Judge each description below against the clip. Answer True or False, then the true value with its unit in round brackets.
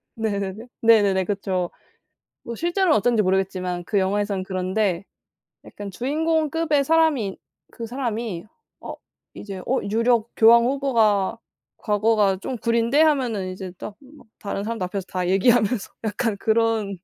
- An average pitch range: True (3.9 semitones)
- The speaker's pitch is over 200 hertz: True (220 Hz)